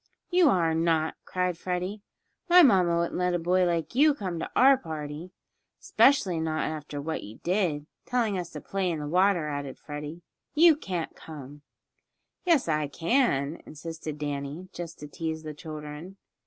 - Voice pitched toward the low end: No, medium, 165 Hz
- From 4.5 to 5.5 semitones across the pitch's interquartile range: No, average, 3.6 semitones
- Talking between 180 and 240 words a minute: No, average, 165 wpm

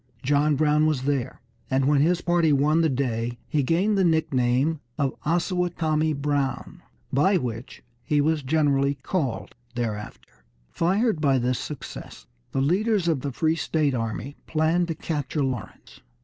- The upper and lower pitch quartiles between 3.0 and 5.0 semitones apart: Yes, average, 3.6 semitones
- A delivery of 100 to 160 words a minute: Yes, average, 150 wpm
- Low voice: No, medium, 150 Hz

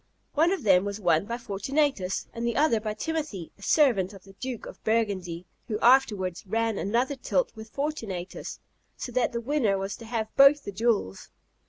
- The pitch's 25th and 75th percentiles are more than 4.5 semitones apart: Yes, average, 5.1 semitones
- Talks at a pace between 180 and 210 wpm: Yes, average, 185 wpm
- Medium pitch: No, high, 225 Hz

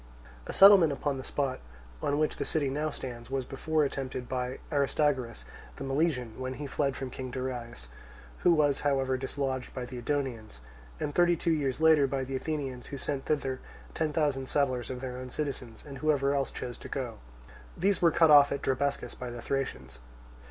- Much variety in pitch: No, narrow, 2.4 semitones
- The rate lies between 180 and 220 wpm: Yes, average, 185 wpm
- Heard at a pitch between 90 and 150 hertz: Yes, low, 135 Hz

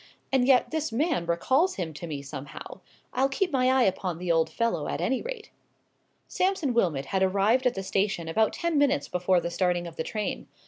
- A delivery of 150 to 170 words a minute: No, average, 200 wpm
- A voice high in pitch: Yes, high, 200 Hz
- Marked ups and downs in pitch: Yes, wide, 7.8 semitones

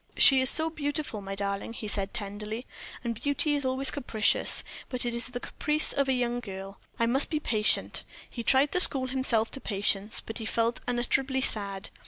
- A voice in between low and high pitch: No, high, 240 Hz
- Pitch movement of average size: Yes, average, 4.1 semitones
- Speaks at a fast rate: No, average, 195 wpm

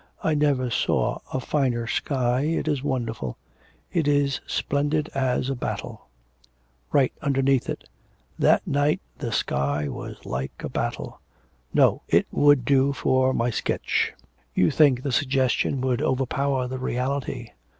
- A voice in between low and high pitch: No, low, 130 Hz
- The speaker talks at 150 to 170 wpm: No, average, 140 wpm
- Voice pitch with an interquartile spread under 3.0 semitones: Yes, narrow, 2.4 semitones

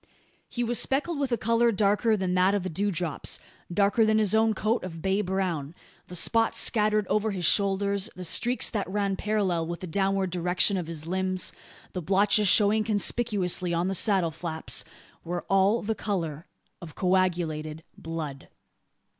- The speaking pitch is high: Yes, high, 195 Hz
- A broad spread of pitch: No, average, 3.4 semitones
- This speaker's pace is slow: No, average, 170 wpm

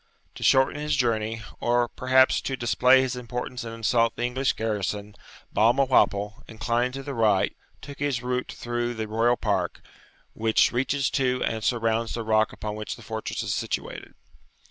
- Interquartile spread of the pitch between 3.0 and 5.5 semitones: No, narrow, 2.4 semitones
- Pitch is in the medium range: No, low, 120 Hz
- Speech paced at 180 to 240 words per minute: No, average, 165 wpm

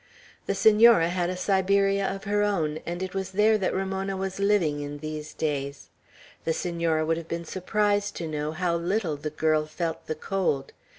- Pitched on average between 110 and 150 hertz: No, medium, 175 Hz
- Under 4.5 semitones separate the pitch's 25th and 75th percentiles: Yes, average, 3.9 semitones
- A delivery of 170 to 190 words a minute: Yes, average, 185 wpm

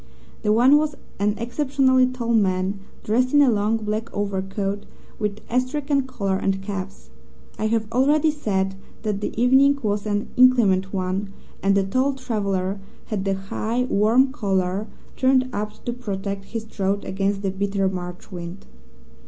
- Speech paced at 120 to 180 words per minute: Yes, average, 150 wpm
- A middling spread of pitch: Yes, average, 4.4 semitones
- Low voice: No, high, 210 Hz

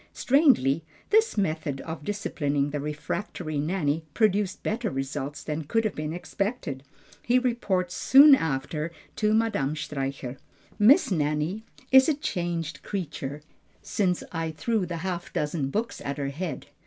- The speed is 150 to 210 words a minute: No, average, 140 wpm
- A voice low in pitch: No, medium, 170 Hz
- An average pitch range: No, wide, 6.2 semitones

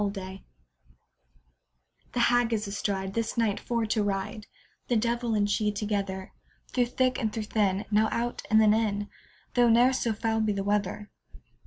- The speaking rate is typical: Yes, average, 170 wpm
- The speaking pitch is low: No, high, 215 Hz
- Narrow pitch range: Yes, narrow, 2.3 semitones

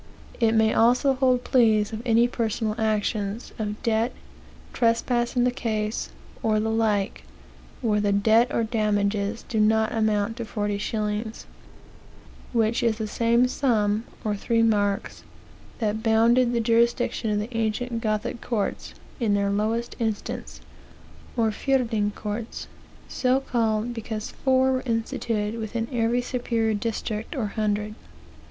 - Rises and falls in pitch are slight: Yes, narrow, 1.9 semitones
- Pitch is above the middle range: Yes, high, 225 Hz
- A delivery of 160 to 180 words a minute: No, slow, 135 wpm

